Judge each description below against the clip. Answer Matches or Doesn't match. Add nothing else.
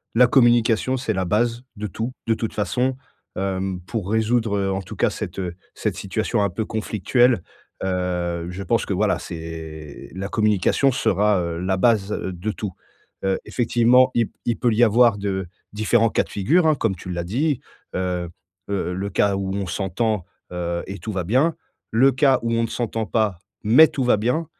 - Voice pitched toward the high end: Doesn't match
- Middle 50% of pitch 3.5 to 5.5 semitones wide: Matches